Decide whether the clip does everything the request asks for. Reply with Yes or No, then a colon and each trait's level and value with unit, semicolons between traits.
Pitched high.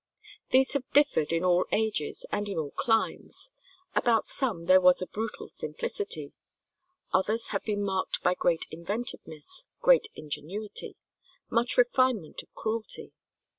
Yes: high, 210 Hz